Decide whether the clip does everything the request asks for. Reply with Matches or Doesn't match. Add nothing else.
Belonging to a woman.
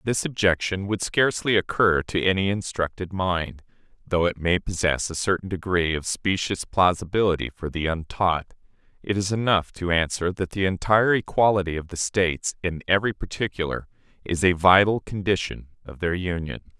Doesn't match